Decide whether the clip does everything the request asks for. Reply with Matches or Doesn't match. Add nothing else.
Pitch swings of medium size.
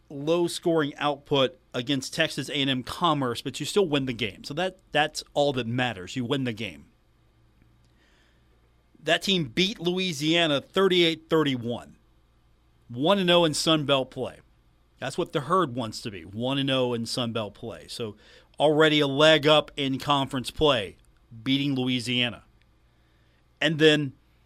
Matches